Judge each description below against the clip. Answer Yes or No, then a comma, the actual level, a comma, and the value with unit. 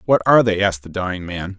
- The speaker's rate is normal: No, fast, 265 wpm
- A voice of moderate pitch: No, very low, 95 Hz